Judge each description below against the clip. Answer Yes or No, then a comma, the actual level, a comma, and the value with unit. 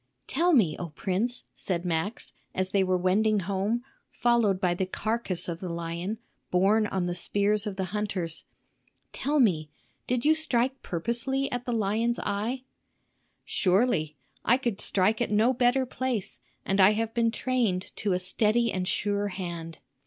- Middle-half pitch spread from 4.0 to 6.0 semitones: Yes, average, 4.5 semitones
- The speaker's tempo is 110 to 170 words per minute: Yes, average, 160 wpm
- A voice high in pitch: Yes, high, 205 Hz